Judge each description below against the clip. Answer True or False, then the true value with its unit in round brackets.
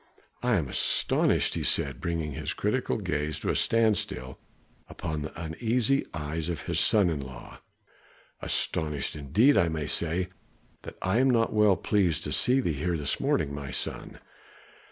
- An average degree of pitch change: False (6.2 semitones)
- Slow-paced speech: False (160 wpm)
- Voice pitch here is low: True (80 Hz)